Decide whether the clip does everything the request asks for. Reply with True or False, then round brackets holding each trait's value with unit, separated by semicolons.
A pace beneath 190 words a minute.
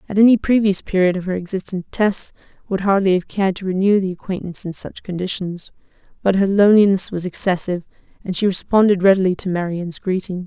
True (180 wpm)